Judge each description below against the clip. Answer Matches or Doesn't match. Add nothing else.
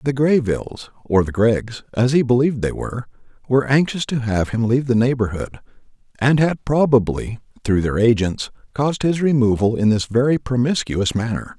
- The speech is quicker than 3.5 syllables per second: Matches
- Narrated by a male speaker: Matches